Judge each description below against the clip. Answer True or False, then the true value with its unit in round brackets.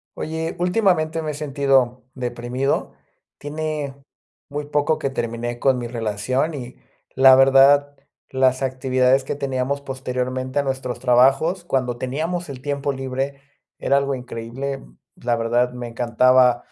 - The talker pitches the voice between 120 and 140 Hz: True (135 Hz)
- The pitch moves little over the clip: True (2.3 semitones)